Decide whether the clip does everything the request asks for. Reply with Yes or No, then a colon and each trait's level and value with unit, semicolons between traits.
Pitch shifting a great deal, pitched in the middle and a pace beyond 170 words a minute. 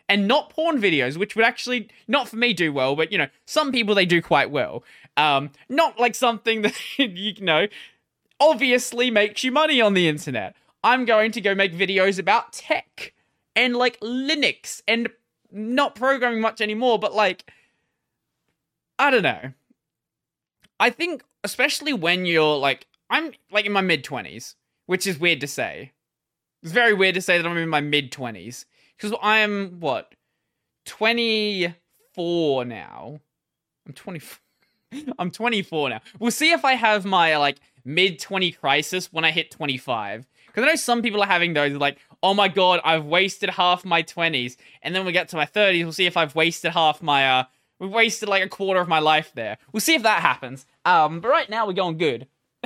No: wide, 6.1 semitones; high, 195 Hz; average, 180 wpm